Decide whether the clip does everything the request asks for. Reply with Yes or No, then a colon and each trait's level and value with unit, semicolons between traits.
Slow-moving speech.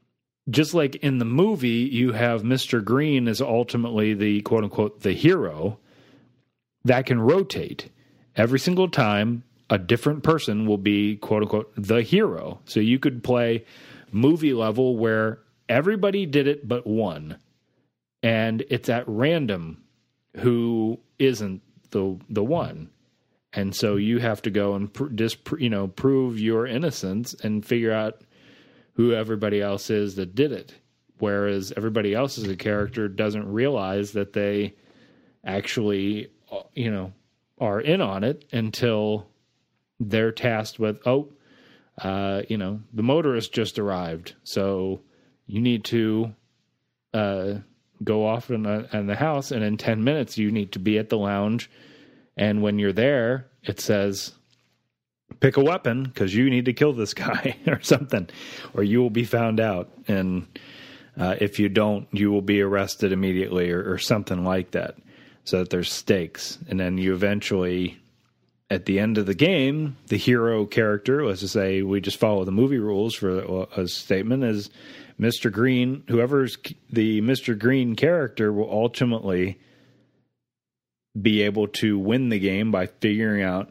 No: average, 155 wpm